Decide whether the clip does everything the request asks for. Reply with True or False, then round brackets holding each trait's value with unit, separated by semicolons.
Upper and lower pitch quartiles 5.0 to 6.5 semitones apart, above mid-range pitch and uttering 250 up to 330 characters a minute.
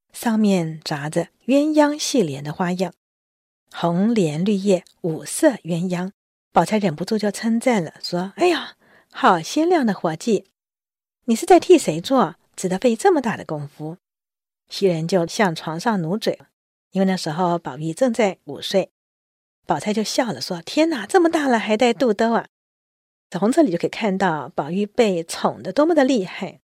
False (5.4 semitones; 195 Hz; 240 characters per minute)